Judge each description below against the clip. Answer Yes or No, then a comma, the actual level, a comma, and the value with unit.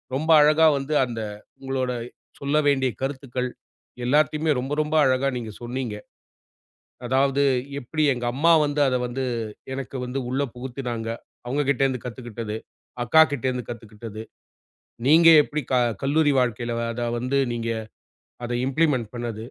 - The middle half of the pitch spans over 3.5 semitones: No, average, 3.0 semitones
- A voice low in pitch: Yes, low, 130 Hz